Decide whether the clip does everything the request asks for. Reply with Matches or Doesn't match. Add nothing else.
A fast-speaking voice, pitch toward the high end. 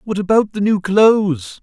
Doesn't match